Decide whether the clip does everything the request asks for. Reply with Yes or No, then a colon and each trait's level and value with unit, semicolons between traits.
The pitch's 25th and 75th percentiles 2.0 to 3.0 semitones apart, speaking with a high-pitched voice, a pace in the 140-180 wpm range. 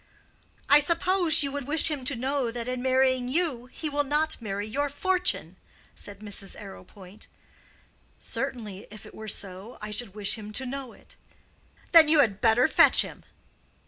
No: wide, 5.5 semitones; very high, 255 Hz; average, 170 wpm